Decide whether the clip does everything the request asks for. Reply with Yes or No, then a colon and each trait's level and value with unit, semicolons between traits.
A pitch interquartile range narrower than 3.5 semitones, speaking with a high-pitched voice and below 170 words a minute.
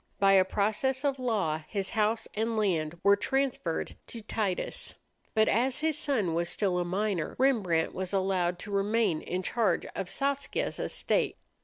No: average, 4.2 semitones; high, 205 Hz; average, 160 wpm